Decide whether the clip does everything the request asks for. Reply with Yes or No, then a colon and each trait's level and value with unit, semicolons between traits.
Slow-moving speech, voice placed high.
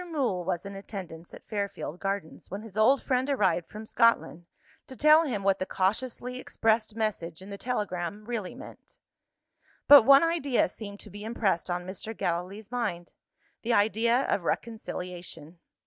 No: average, 160 wpm; high, 210 Hz